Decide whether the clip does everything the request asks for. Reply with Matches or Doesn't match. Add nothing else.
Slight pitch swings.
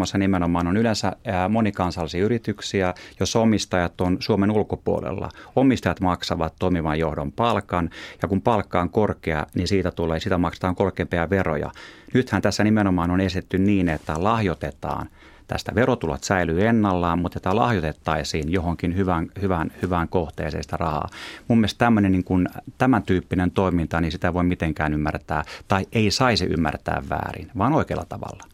Doesn't match